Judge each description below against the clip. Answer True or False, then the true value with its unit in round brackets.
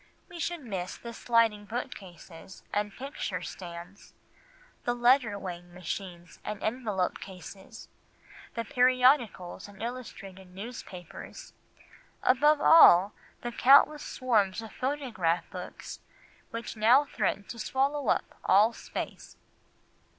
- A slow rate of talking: True (105 wpm)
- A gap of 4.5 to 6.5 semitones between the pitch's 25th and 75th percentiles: True (5.2 semitones)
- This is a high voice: True (215 Hz)